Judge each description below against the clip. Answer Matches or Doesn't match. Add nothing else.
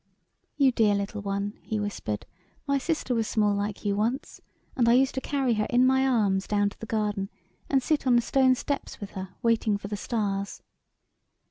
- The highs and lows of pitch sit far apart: Doesn't match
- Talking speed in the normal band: Doesn't match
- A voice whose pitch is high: Matches